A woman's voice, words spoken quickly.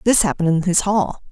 Yes: female; fast, 230 wpm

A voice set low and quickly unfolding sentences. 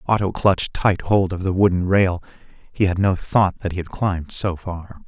Yes: very low, 95 Hz; fast, 215 wpm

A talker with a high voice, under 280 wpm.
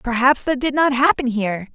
Yes: very high, 250 Hz; fast, 205 wpm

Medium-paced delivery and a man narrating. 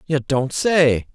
Yes: average, 160 wpm; male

